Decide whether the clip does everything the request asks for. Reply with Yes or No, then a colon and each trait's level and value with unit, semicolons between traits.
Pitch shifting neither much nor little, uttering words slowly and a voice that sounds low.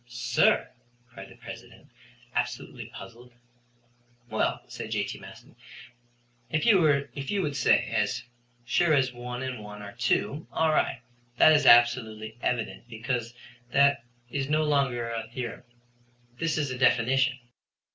Yes: average, 3.2 semitones; slow, 130 wpm; low, 125 Hz